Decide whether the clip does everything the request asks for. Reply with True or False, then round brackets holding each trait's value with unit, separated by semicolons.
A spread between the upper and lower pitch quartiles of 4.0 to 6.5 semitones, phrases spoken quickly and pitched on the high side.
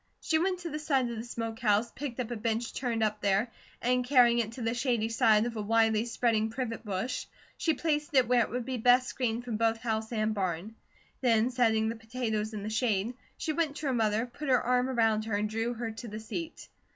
False (2.4 semitones; 235 wpm; 230 Hz)